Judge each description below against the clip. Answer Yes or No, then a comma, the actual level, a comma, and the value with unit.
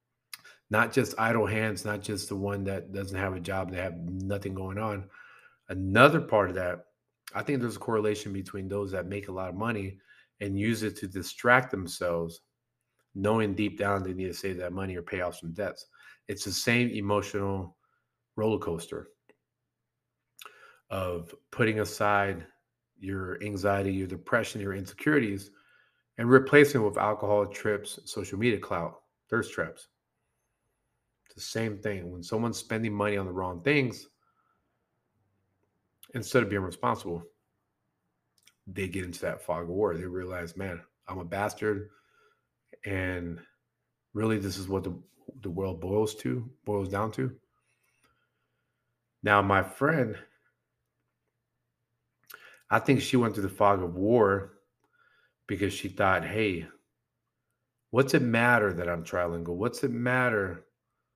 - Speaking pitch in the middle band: No, low, 100 Hz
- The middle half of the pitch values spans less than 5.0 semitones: Yes, average, 3.0 semitones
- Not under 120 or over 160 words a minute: Yes, average, 145 wpm